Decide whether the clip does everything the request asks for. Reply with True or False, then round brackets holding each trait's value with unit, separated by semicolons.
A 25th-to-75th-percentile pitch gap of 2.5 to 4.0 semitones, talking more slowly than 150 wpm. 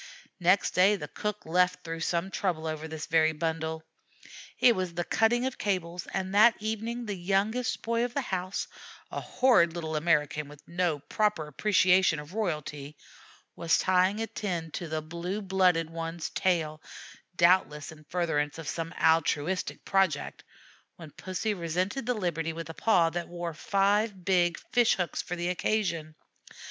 False (3.5 semitones; 160 wpm)